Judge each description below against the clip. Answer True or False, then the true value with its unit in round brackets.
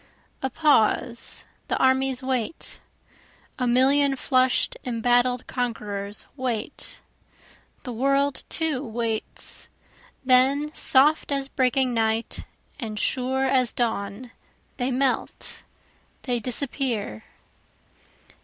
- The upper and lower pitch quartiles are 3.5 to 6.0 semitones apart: False (2.4 semitones)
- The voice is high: True (255 Hz)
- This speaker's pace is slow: True (90 wpm)